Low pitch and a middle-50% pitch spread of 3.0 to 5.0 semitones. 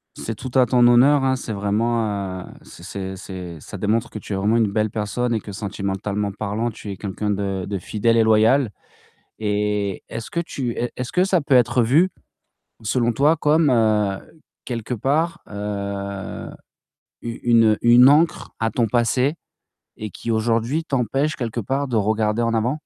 Yes: low, 115 Hz; average, 3.5 semitones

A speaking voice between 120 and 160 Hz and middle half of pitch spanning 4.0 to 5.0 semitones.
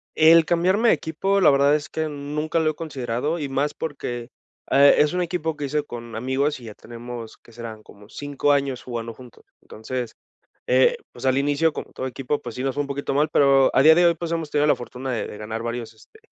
Yes: medium, 140 Hz; average, 4.3 semitones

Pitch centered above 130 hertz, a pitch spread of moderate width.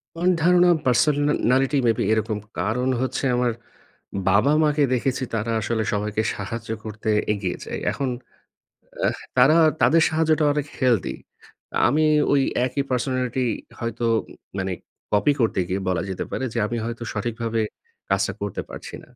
No: low, 125 Hz; average, 4.6 semitones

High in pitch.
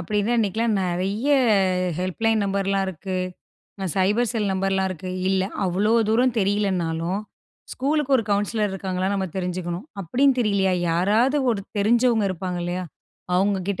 Yes: high, 195 Hz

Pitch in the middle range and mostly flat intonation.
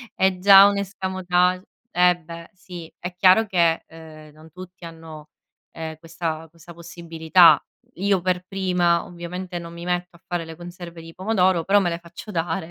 Yes: medium, 175 Hz; narrow, 1.9 semitones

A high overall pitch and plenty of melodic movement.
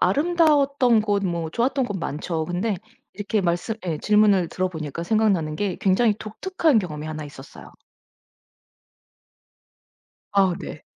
No: high, 195 Hz; average, 4.9 semitones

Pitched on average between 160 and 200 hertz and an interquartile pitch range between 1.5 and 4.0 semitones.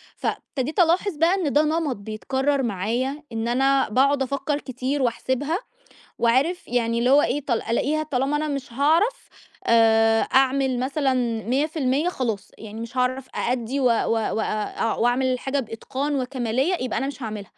No: very high, 265 Hz; average, 3.5 semitones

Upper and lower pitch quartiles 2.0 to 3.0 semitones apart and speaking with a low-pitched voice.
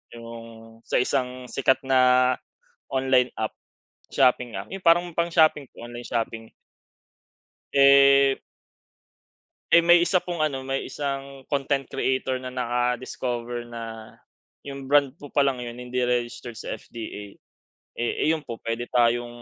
Yes: narrow, 2.5 semitones; low, 130 Hz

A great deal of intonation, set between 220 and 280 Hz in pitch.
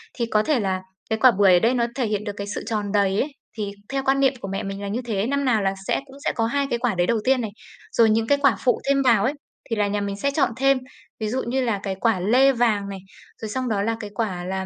No: average, 4.2 semitones; high, 225 Hz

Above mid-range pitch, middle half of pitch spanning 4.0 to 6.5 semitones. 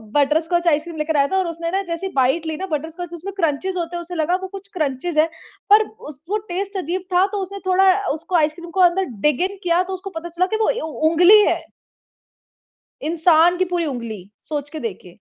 No: very high, 340 Hz; average, 3.2 semitones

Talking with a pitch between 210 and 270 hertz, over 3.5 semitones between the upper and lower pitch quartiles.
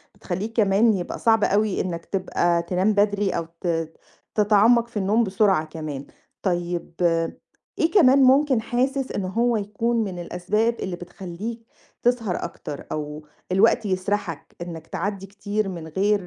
No: high, 200 Hz; average, 4.3 semitones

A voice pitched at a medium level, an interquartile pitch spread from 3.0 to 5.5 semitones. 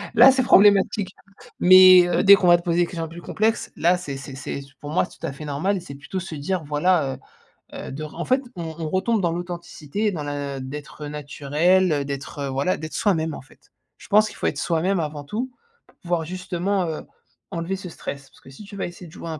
Yes: medium, 170 Hz; average, 4.2 semitones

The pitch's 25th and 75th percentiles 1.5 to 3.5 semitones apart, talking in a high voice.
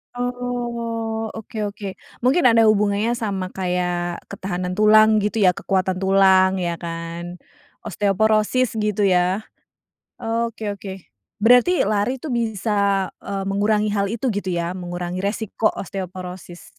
Yes: average, 3.1 semitones; high, 200 Hz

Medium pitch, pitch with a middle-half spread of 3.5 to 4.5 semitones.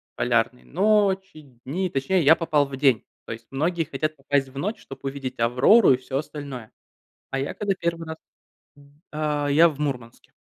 Yes: medium, 145 Hz; average, 3.8 semitones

